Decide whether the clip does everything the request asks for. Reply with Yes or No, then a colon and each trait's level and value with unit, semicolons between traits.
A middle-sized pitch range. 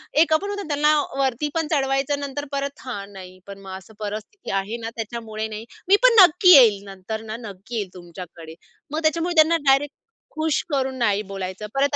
No: wide, 6.6 semitones